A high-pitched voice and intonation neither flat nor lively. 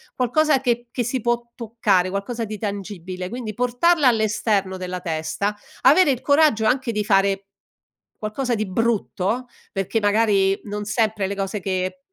Yes: high, 215 Hz; average, 3.7 semitones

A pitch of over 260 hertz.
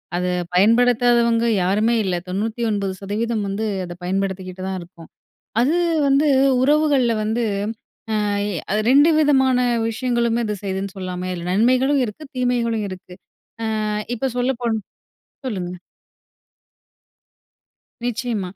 No: high, 225 Hz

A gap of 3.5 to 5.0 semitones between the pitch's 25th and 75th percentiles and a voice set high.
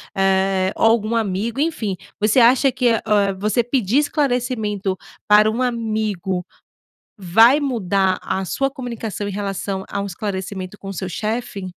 Yes: average, 3.8 semitones; high, 210 Hz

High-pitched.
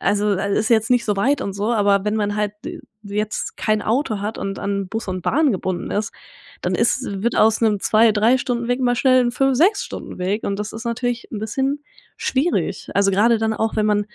Yes: high, 220 Hz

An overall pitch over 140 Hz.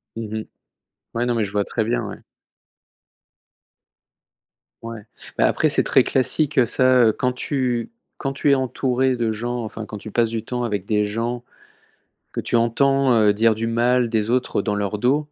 No: low, 115 Hz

